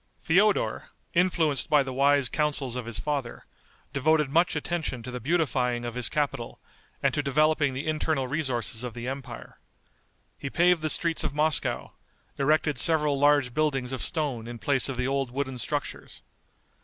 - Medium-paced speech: Yes, average, 165 wpm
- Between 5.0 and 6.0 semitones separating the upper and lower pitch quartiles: No, average, 3.4 semitones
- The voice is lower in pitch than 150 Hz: Yes, medium, 140 Hz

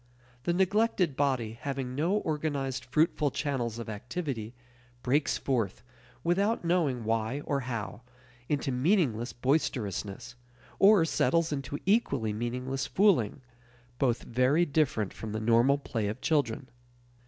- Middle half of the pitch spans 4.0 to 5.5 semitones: Yes, average, 5.1 semitones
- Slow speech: Yes, slow, 120 wpm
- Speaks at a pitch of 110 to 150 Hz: Yes, low, 135 Hz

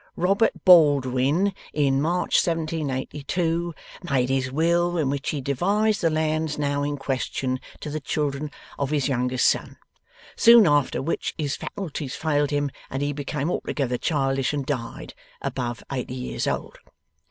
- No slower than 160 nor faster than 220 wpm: No, average, 145 wpm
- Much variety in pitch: No, average, 3.3 semitones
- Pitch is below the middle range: No, medium, 145 Hz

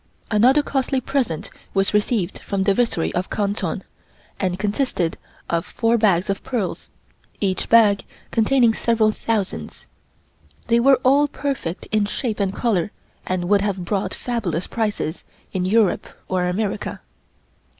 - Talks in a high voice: Yes, high, 210 Hz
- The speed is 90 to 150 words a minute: Yes, slow, 135 wpm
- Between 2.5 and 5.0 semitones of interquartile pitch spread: Yes, average, 3.8 semitones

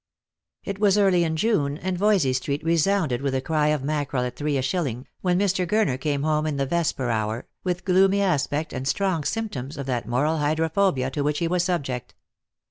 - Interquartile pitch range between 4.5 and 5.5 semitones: Yes, average, 5.1 semitones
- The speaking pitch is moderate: Yes, medium, 155 Hz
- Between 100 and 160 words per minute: No, average, 200 wpm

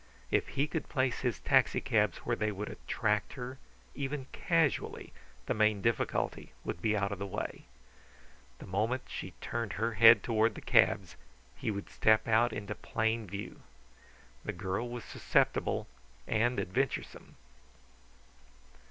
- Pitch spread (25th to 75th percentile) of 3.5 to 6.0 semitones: No, average, 2.9 semitones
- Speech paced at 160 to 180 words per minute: No, average, 140 wpm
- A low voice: Yes, low, 110 Hz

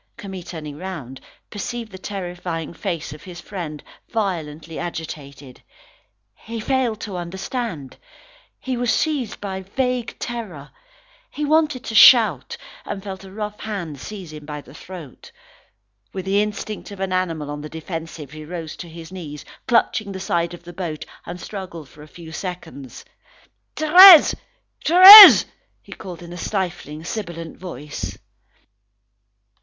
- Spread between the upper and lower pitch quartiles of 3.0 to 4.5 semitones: No, average, 4.9 semitones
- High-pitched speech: No, medium, 180 Hz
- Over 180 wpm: No, average, 145 wpm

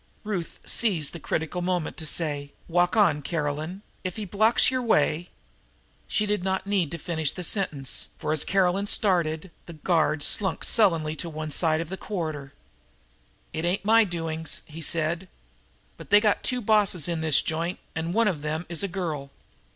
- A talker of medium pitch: Yes, medium, 170 Hz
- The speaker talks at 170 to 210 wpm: Yes, average, 180 wpm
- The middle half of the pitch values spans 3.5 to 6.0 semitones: Yes, average, 3.8 semitones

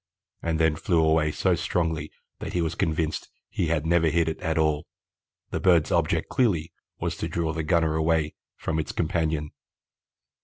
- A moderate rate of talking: Yes, average, 170 wpm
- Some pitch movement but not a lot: No, narrow, 1.2 semitones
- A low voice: Yes, very low, 80 Hz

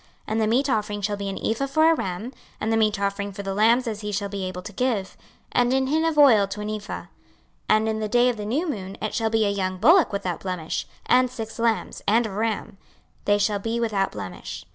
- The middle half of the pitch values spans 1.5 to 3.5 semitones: Yes, average, 2.8 semitones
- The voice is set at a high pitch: Yes, high, 215 Hz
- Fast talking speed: Yes, fast, 250 wpm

